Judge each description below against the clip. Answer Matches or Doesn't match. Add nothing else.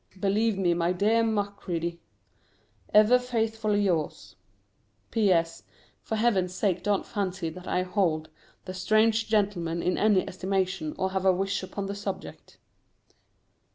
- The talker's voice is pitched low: Doesn't match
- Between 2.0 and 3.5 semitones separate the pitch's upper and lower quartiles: Matches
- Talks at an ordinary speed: Doesn't match